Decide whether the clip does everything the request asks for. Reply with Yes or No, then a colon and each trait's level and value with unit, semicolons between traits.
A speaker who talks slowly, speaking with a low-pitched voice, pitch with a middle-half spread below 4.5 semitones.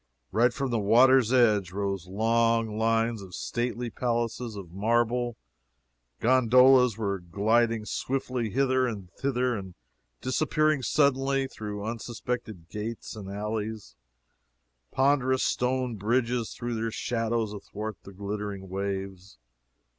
Yes: slow, 115 wpm; low, 115 Hz; average, 3.4 semitones